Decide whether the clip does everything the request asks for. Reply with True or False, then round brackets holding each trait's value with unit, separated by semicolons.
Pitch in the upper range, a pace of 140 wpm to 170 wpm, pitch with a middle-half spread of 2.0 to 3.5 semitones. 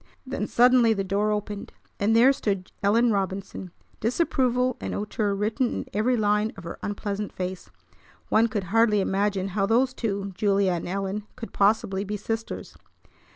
True (210 Hz; 155 wpm; 2.4 semitones)